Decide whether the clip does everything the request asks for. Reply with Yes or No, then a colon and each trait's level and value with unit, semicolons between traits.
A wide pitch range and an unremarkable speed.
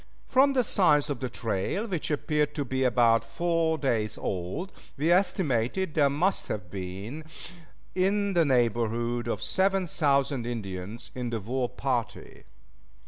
Yes: wide, 6.4 semitones; average, 145 wpm